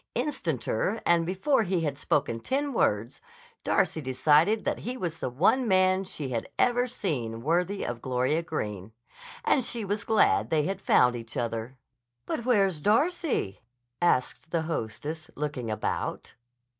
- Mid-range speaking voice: Yes, medium, 165 Hz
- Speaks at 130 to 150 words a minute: Yes, average, 145 wpm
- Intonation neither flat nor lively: No, wide, 8.3 semitones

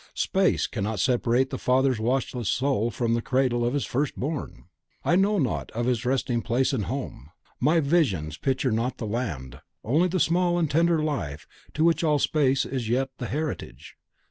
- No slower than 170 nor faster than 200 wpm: Yes, average, 185 wpm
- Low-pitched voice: Yes, low, 130 Hz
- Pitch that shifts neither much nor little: Yes, average, 4.4 semitones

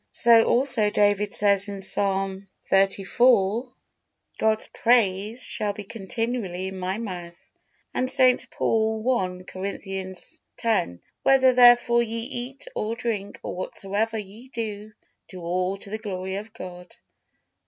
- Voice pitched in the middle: No, high, 210 Hz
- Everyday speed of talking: No, slow, 130 wpm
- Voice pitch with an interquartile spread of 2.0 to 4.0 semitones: Yes, average, 3.3 semitones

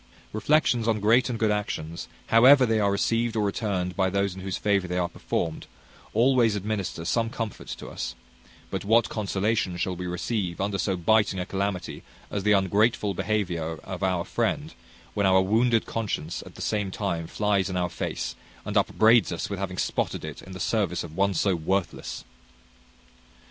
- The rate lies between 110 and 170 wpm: No, average, 180 wpm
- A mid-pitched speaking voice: No, low, 100 Hz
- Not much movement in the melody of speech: No, average, 3.2 semitones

